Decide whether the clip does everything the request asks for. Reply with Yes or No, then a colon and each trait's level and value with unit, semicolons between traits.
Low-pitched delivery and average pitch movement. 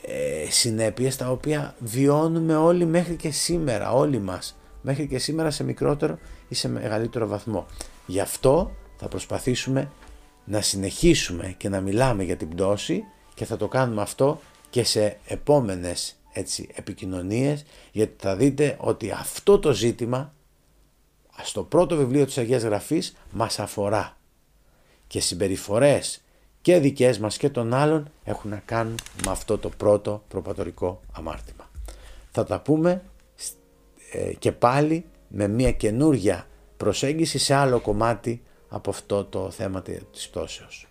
No: low, 115 Hz; wide, 6.2 semitones